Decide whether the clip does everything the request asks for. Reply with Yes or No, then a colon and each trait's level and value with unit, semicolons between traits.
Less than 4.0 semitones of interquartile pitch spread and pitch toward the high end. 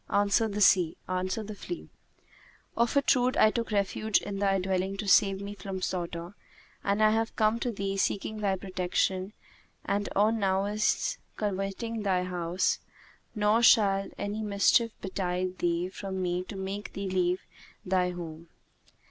Yes: narrow, 2.4 semitones; high, 195 Hz